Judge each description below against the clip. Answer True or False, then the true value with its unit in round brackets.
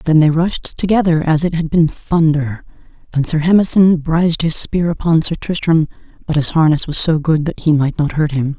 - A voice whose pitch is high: False (160 Hz)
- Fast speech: True (210 wpm)